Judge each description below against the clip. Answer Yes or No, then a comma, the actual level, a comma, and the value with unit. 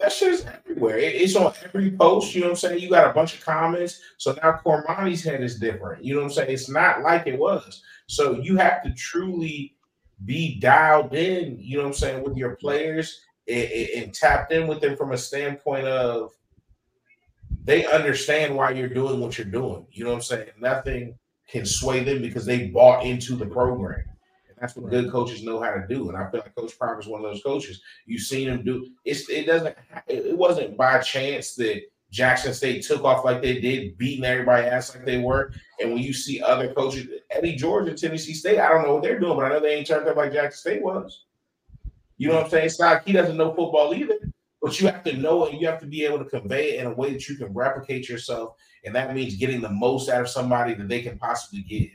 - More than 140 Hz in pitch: No, low, 135 Hz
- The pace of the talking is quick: Yes, fast, 240 wpm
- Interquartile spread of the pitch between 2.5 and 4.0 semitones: No, average, 4.6 semitones